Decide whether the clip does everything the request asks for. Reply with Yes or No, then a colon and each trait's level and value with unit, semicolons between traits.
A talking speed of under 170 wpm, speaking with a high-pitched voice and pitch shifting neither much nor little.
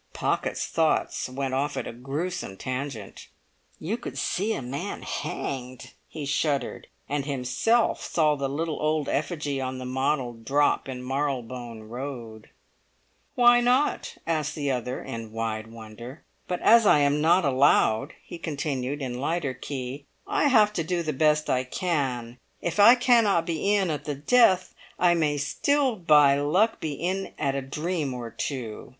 No: average, 160 wpm; medium, 145 Hz; average, 4.9 semitones